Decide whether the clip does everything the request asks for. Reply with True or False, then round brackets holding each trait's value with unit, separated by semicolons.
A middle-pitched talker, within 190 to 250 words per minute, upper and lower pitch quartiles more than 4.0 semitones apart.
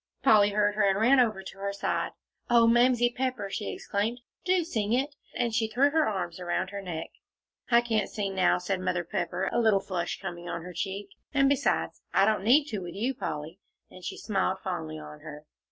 False (205 Hz; 205 wpm; 4.6 semitones)